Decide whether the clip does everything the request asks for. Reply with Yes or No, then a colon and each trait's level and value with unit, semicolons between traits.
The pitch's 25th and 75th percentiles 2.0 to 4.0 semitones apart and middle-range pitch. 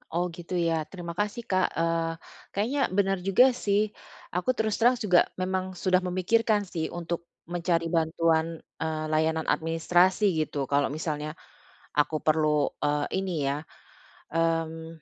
Yes: average, 2.9 semitones; medium, 170 Hz